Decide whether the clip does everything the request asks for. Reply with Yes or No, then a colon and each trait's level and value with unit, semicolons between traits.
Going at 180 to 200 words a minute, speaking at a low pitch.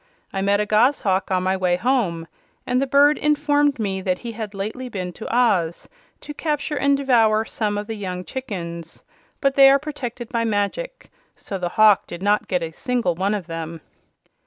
No: average, 190 wpm; high, 215 Hz